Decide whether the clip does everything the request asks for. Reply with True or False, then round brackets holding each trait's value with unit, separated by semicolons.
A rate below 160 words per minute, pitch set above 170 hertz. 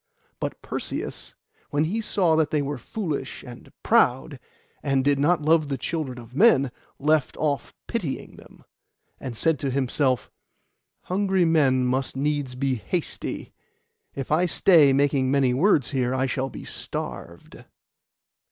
False (145 wpm; 140 Hz)